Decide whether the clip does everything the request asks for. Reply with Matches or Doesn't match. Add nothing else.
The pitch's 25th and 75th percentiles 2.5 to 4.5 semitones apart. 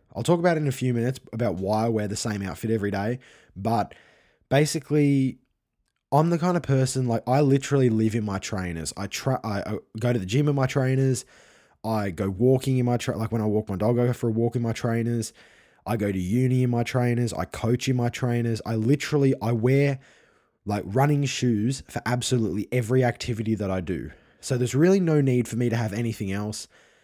Matches